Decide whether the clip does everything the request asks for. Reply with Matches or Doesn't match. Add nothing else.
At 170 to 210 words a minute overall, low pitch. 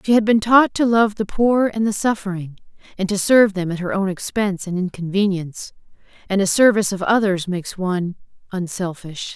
Doesn't match